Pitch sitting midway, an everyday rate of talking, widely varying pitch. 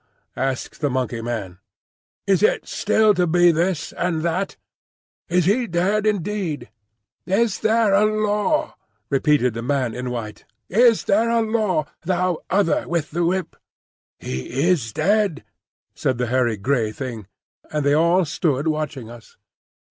Yes: medium, 170 Hz; average, 145 wpm; wide, 7.4 semitones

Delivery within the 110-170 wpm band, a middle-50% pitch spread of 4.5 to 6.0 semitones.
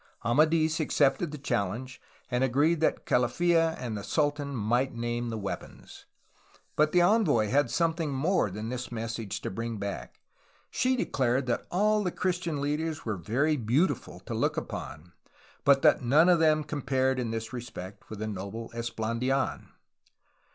Yes: average, 155 wpm; wide, 5.4 semitones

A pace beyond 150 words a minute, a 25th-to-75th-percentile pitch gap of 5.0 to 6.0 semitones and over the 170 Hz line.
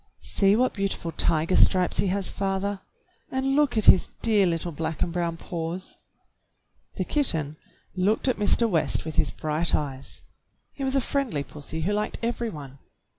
Yes: average, 170 wpm; average, 5.3 semitones; medium, 185 Hz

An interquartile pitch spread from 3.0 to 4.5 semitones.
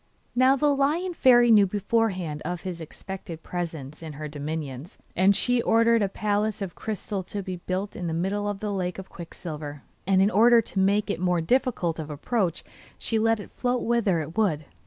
No: average, 5.1 semitones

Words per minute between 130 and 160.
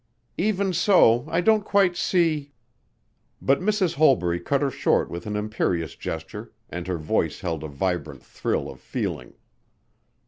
Yes: average, 150 wpm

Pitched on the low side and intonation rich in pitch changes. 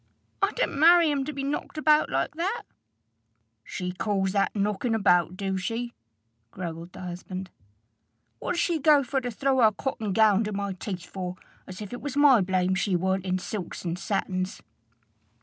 No: high, 205 Hz; wide, 6.6 semitones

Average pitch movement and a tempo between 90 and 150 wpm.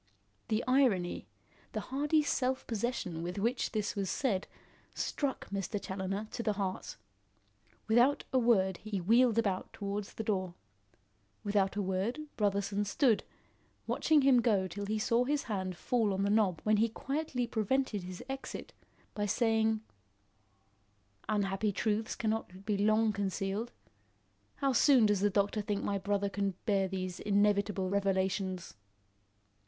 Yes: average, 3.0 semitones; average, 140 wpm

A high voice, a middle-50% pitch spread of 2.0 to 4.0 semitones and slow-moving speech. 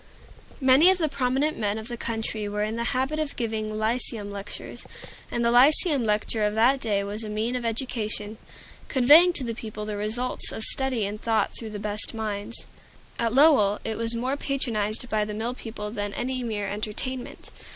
No: high, 225 Hz; average, 3.2 semitones; average, 190 wpm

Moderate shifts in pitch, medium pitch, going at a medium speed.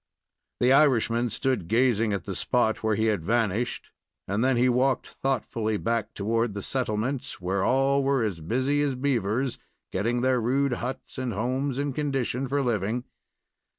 No: average, 3.4 semitones; low, 120 Hz; average, 160 wpm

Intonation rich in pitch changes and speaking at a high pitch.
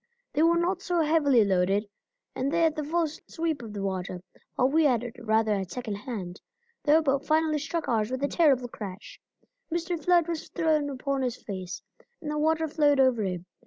Yes: wide, 6.6 semitones; very high, 280 Hz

